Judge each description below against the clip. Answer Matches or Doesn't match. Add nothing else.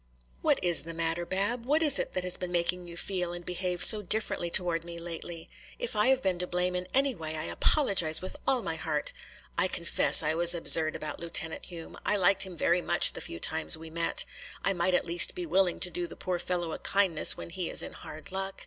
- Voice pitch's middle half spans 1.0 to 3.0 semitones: Matches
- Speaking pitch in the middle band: Matches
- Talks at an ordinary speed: Doesn't match